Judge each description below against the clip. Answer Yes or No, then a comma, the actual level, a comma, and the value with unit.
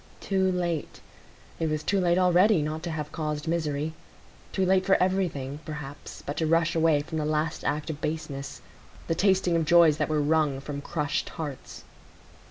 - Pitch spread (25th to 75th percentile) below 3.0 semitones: Yes, narrow, 2.6 semitones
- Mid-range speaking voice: Yes, medium, 160 Hz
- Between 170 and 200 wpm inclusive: Yes, average, 175 wpm